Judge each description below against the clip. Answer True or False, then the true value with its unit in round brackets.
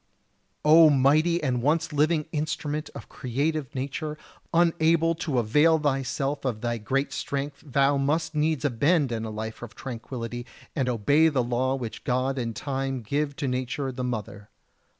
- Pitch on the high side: False (135 Hz)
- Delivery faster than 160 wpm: False (150 wpm)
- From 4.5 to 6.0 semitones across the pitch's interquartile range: False (3.7 semitones)